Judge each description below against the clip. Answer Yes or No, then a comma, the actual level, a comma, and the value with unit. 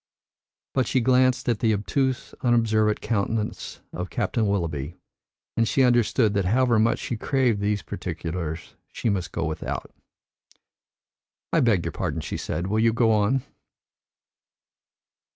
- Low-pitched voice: Yes, low, 110 Hz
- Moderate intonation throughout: Yes, average, 3.4 semitones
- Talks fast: No, average, 140 wpm